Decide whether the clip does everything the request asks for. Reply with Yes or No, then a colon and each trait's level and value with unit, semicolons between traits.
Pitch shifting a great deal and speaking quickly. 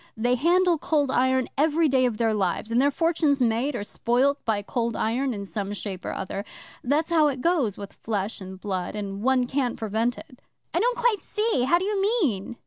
Yes: wide, 6.1 semitones; fast, 210 wpm